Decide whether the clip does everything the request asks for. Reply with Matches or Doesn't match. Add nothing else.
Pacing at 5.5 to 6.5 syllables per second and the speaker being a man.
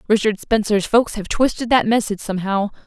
Doesn't match